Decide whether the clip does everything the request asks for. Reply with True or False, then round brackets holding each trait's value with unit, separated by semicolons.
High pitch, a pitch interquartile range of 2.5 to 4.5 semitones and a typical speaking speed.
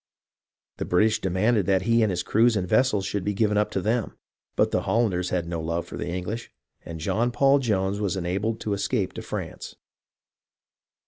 False (100 Hz; 3.6 semitones; 190 wpm)